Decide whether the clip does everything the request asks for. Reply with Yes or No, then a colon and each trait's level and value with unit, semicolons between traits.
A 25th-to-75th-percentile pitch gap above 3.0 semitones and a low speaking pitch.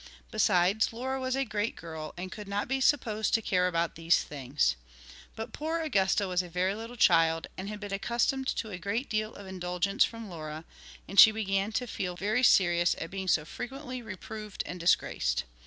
No: average, 4.2 semitones; high, 200 Hz